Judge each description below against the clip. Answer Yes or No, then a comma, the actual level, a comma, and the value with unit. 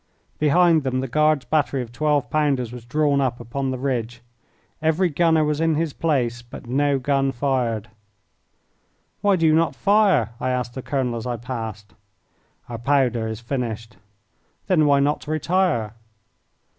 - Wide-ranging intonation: No, average, 4.1 semitones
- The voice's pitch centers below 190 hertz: Yes, low, 135 Hz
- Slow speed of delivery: No, average, 155 wpm